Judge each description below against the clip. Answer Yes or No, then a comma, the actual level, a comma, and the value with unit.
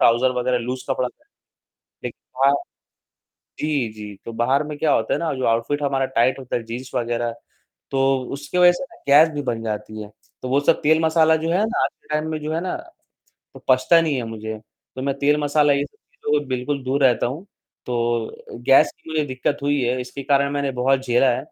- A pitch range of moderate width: Yes, average, 3.6 semitones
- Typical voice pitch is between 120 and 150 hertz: Yes, low, 135 Hz